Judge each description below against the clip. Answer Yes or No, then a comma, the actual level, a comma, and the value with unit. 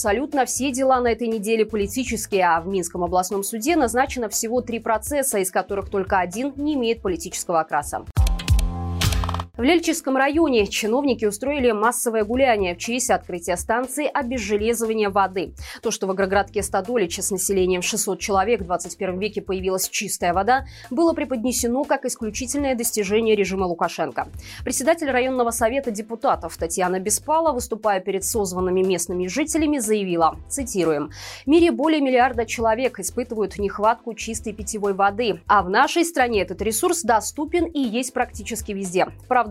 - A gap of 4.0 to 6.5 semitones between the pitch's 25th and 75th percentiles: Yes, average, 5.0 semitones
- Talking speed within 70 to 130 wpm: No, average, 145 wpm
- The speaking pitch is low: No, high, 220 Hz